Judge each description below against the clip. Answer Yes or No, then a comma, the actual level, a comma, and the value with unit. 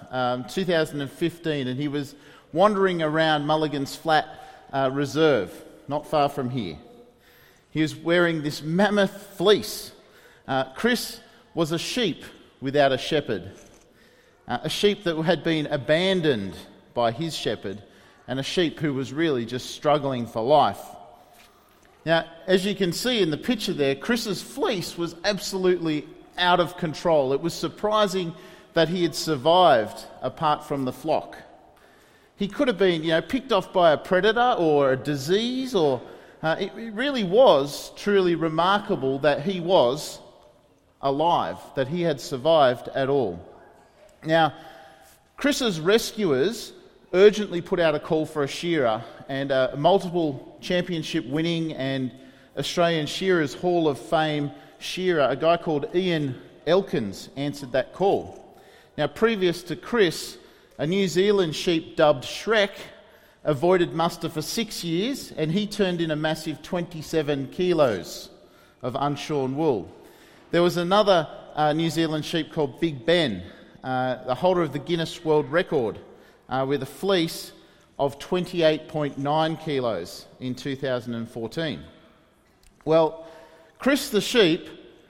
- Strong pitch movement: No, average, 4.3 semitones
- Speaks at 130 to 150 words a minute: Yes, average, 140 wpm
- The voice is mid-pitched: Yes, medium, 160 Hz